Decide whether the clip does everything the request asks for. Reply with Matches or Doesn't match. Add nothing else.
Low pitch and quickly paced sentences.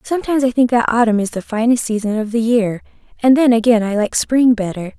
Doesn't match